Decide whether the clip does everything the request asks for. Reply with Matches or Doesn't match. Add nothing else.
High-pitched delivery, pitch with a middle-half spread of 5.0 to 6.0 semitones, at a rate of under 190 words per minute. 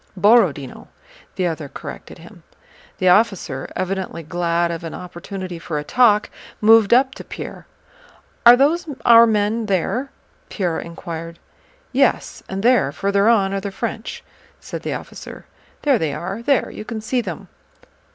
Matches